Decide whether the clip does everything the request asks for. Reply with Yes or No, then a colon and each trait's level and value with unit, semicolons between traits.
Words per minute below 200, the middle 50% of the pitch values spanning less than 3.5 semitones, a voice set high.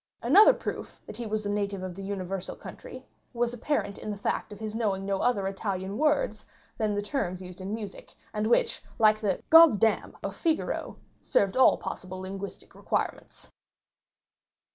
Yes: average, 165 wpm; average, 2.8 semitones; high, 205 Hz